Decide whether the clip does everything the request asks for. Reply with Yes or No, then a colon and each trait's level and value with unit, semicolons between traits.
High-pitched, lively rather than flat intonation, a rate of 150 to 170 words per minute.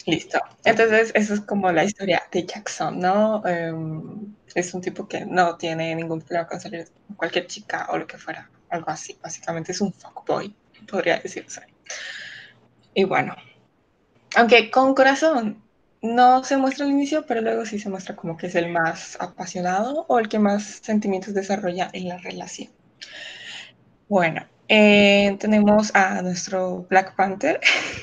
No: high, 195 Hz; average, 3.5 semitones; average, 155 wpm